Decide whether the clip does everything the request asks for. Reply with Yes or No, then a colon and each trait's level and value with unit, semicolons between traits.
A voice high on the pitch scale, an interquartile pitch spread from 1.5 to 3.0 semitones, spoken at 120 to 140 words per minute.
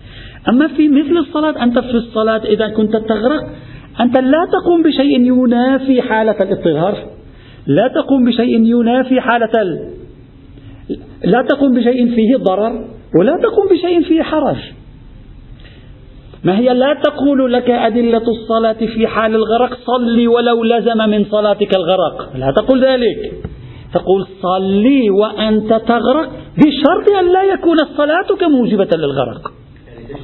No: high, 235 Hz; average, 4.6 semitones; average, 125 wpm